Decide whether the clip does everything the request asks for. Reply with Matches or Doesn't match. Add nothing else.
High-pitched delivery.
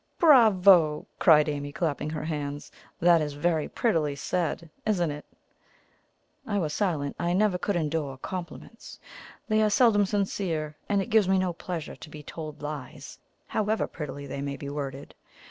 Doesn't match